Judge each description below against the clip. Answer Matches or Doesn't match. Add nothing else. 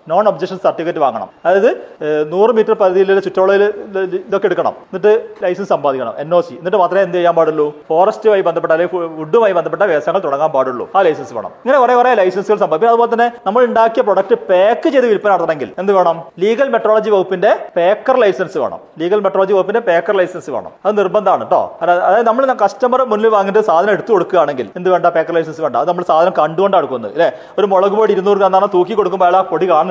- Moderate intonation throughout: Matches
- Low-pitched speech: Doesn't match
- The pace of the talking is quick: Matches